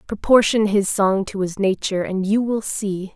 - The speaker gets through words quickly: No, average, 190 wpm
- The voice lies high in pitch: Yes, high, 200 Hz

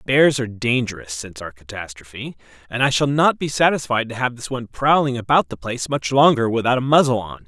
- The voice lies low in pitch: Yes, low, 120 Hz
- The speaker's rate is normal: Yes, average, 195 wpm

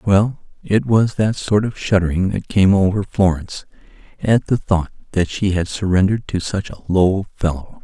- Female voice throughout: No, male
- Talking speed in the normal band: Yes, average, 175 wpm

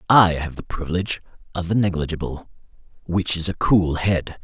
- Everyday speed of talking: Yes, average, 150 wpm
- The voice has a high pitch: No, very low, 85 Hz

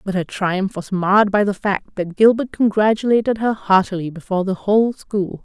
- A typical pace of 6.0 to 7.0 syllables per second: No, 5.4 syllables/s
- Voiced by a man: No, female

